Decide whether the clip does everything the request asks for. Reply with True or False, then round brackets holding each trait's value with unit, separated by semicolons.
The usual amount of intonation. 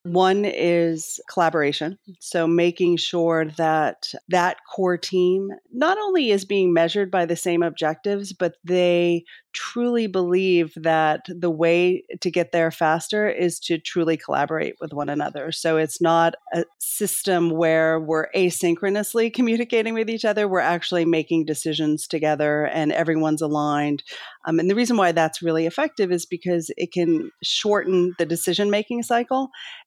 True (3.1 semitones)